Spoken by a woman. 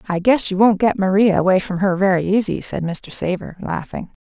Yes: female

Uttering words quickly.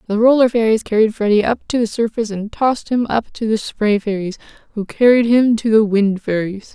Yes: fast, 215 wpm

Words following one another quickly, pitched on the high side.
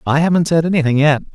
No: fast, 225 wpm; medium, 155 Hz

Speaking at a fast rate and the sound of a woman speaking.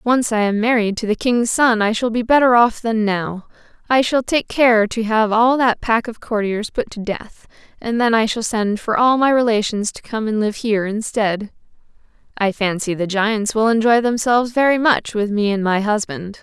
Yes: fast, 210 wpm; female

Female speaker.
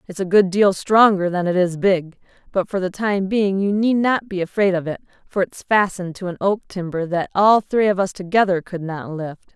Yes: female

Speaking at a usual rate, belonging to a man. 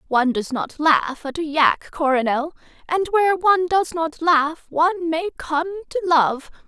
No: average, 170 wpm; female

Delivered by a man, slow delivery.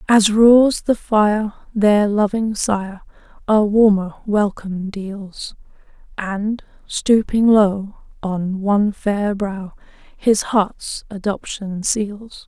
No: female; slow, 105 wpm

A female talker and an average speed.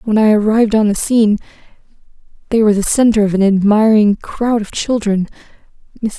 Yes: female; average, 155 wpm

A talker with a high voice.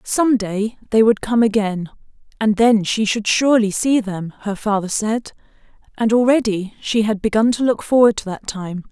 Yes: high, 215 Hz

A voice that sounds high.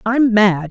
Yes: high, 210 Hz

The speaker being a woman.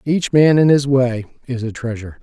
No: male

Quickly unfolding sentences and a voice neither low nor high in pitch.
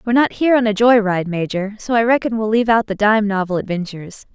No: fast, 250 wpm; high, 215 Hz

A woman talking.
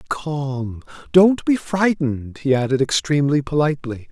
No: male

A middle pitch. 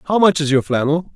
Yes: medium, 155 Hz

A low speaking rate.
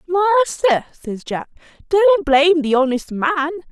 Yes: slow, 130 wpm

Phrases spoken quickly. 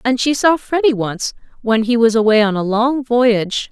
Yes: fast, 210 wpm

